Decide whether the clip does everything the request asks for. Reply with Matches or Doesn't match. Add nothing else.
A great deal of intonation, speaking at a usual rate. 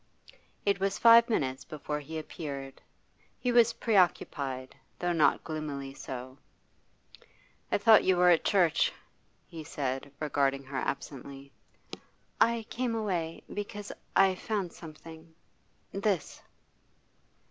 Doesn't match